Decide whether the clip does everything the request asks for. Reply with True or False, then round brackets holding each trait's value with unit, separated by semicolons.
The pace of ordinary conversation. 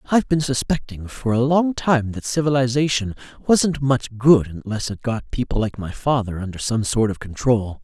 True (185 wpm)